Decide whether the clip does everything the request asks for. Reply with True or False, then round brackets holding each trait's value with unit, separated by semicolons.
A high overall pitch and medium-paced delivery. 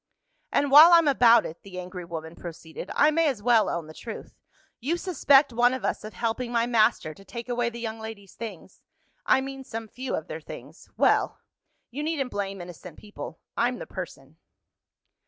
True (230 Hz; 190 wpm)